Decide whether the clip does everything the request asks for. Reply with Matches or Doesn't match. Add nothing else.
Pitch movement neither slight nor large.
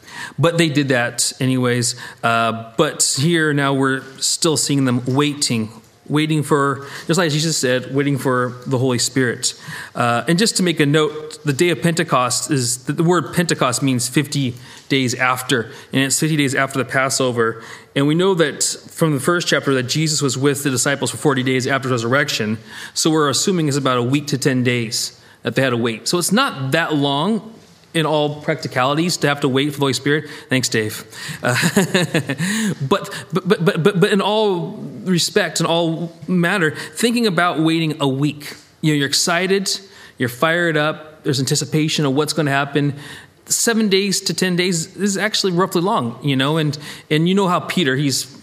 Matches